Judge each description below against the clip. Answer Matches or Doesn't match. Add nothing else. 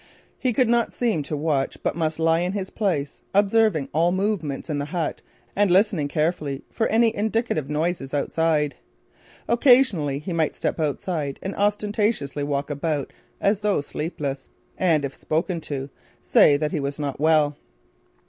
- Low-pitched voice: Doesn't match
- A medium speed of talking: Matches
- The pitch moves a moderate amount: Doesn't match